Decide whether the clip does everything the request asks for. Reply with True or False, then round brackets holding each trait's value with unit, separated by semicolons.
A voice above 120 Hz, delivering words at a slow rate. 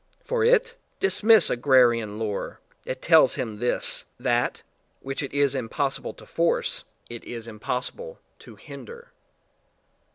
True (135 Hz; 125 wpm)